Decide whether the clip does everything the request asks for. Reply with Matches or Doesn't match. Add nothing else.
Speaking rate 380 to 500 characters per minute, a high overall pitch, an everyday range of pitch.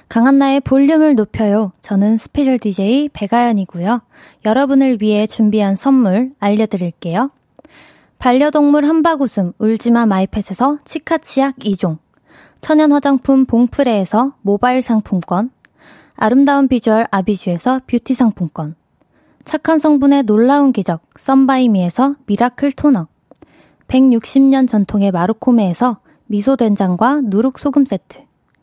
Doesn't match